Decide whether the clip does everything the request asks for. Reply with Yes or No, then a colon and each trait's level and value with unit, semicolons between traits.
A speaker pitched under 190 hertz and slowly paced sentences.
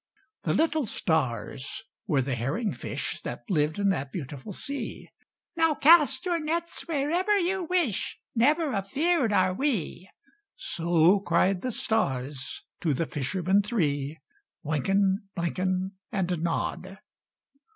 No: high, 195 Hz; slow, 120 wpm